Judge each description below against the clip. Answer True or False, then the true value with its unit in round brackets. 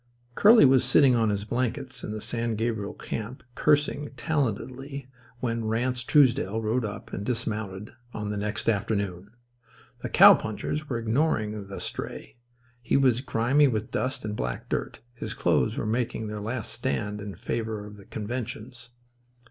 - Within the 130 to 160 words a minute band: True (155 wpm)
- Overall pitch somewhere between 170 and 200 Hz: False (115 Hz)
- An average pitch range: True (3.4 semitones)